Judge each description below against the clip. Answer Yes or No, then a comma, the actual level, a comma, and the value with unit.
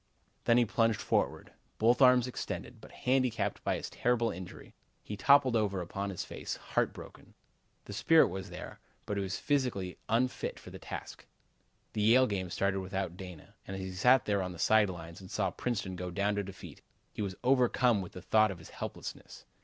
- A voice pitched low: Yes, low, 100 Hz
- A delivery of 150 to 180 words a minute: No, average, 195 wpm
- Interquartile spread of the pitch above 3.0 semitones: Yes, average, 4.4 semitones